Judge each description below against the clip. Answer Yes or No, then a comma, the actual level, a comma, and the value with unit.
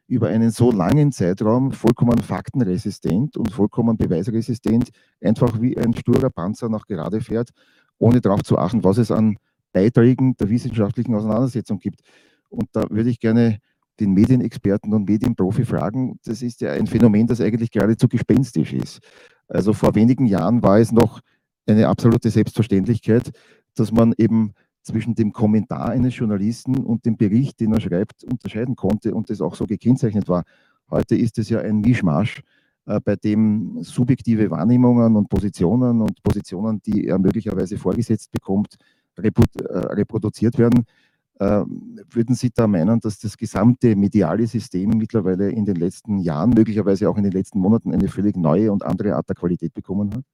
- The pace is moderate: Yes, average, 160 wpm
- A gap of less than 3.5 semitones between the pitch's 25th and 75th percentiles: Yes, narrow, 2.5 semitones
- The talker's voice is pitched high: No, low, 110 Hz